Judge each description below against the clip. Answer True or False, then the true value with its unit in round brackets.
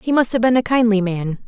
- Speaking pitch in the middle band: False (225 Hz)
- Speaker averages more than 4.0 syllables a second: True (5.6 syllables/s)